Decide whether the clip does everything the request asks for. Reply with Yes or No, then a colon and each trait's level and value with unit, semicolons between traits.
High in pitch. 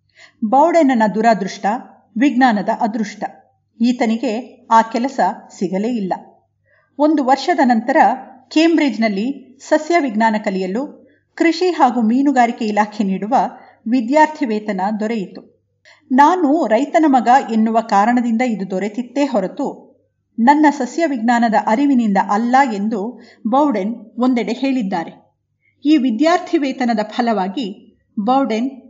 Yes: high, 245 Hz